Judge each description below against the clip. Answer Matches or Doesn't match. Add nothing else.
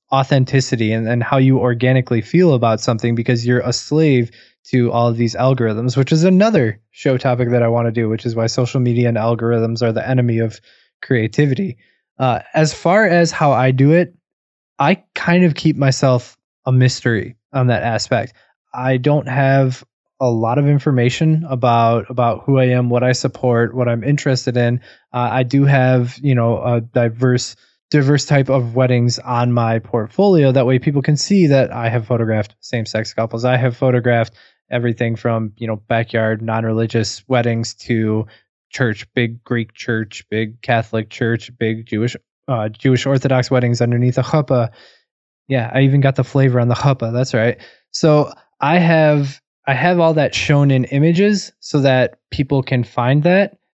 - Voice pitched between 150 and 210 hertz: Doesn't match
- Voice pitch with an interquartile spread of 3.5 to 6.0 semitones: Doesn't match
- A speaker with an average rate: Matches